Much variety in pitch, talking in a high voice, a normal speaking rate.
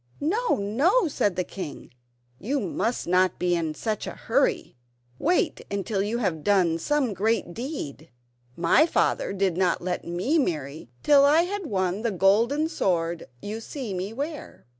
Yes: wide, 7.9 semitones; high, 205 Hz; average, 160 wpm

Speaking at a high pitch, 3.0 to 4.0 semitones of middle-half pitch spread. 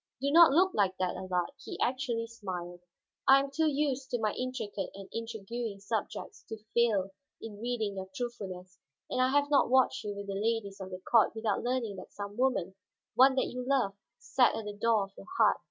No: high, 225 Hz; average, 4.5 semitones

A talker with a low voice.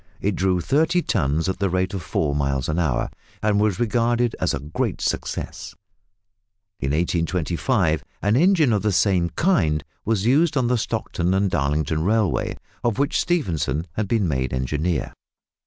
Yes: very low, 95 Hz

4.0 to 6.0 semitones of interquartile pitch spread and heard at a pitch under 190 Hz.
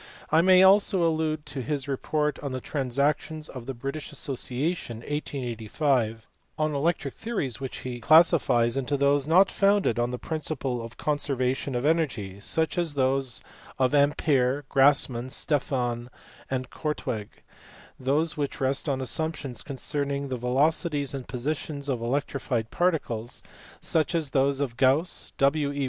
No: average, 3.3 semitones; medium, 140 Hz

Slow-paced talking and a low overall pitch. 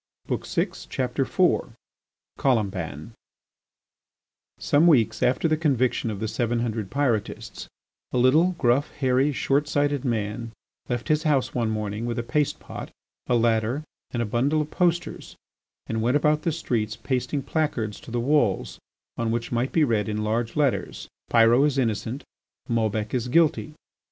No: average, 160 wpm; low, 120 Hz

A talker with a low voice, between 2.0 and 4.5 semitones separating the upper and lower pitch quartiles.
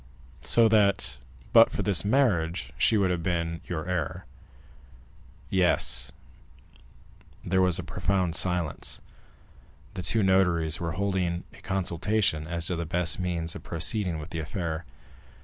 Yes: very low, 90 Hz; narrow, 2.5 semitones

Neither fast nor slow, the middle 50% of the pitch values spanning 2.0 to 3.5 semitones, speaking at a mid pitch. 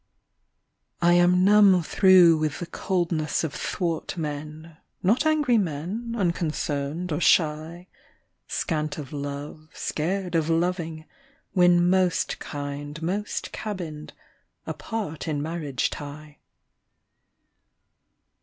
No: slow, 105 wpm; average, 3.1 semitones; medium, 165 Hz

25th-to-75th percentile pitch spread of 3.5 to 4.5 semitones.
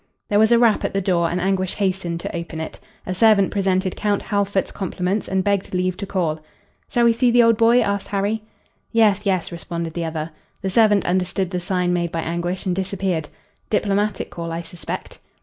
No: average, 2.8 semitones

